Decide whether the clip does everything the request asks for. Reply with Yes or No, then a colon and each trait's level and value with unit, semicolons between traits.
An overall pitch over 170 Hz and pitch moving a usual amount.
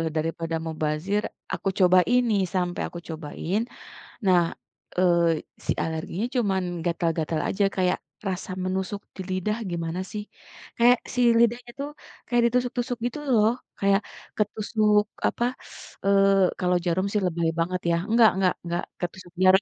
Yes: medium, 185 Hz; average, 3.6 semitones